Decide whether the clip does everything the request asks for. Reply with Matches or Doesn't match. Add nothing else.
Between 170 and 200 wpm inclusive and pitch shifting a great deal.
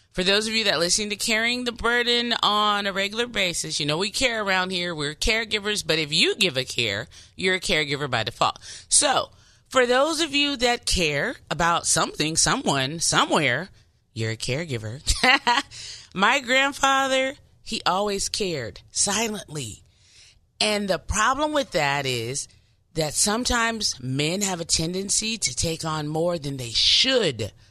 Doesn't match